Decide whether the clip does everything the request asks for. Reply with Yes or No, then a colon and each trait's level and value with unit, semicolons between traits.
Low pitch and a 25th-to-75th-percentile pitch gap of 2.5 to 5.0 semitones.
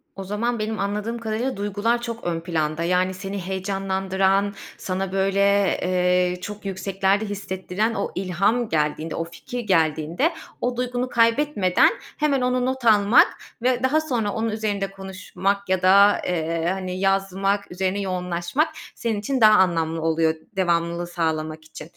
No: high, 195 Hz; average, 3.4 semitones